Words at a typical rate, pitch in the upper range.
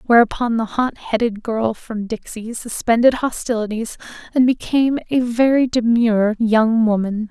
No: slow, 130 wpm; high, 230 Hz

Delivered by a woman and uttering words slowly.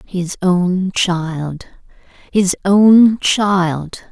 Yes: female; slow, 90 wpm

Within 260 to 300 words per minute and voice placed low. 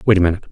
No: fast, 350 wpm; very low, 95 Hz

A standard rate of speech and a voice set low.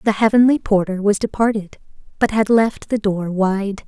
No: average, 170 wpm; high, 210 Hz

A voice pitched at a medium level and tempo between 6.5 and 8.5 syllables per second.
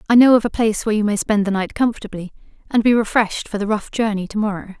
No: high, 215 Hz; 7.1 syllables/s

